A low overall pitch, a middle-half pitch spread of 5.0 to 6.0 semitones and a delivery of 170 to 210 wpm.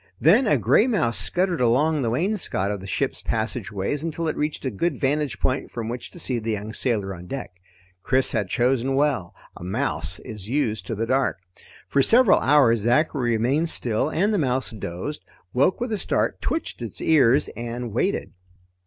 Yes: low, 125 Hz; wide, 5.4 semitones; average, 185 wpm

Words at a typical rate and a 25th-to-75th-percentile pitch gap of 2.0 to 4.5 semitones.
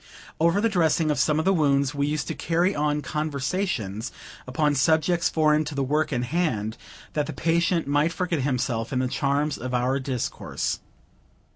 Yes: average, 175 wpm; average, 3.7 semitones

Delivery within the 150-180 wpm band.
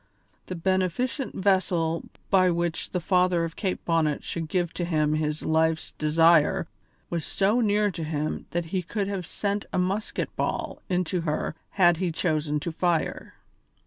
Yes: average, 160 wpm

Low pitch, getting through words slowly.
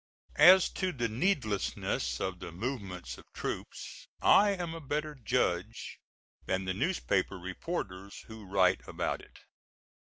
Yes: low, 110 Hz; slow, 130 wpm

